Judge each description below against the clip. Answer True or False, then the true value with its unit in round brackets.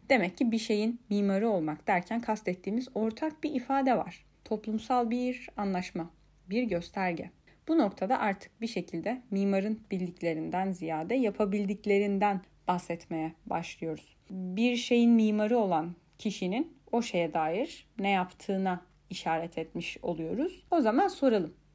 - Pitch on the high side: True (205 Hz)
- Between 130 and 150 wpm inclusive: False (120 wpm)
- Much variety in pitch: False (4.7 semitones)